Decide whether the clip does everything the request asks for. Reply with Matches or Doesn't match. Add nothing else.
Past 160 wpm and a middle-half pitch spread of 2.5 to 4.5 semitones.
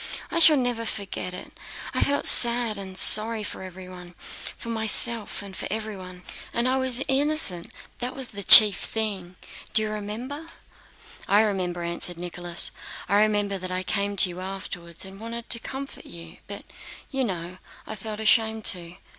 Matches